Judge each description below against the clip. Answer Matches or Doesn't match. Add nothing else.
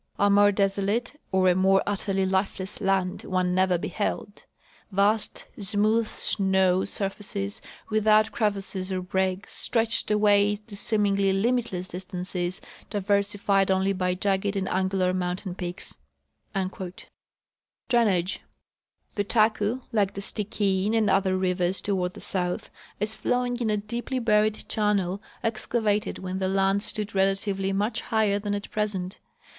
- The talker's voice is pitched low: Doesn't match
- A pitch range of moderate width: Doesn't match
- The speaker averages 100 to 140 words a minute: Matches